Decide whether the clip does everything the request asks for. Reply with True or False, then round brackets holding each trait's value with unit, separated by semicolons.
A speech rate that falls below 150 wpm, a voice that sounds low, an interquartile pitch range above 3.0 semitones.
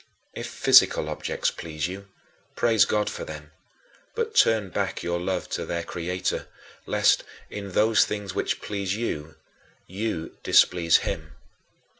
True (135 wpm; 90 Hz; 4.1 semitones)